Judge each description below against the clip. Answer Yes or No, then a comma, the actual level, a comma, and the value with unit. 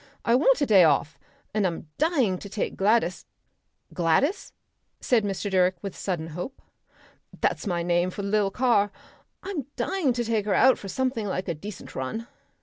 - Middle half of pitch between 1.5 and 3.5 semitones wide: No, average, 5.0 semitones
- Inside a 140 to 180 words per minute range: Yes, average, 175 wpm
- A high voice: Yes, high, 205 Hz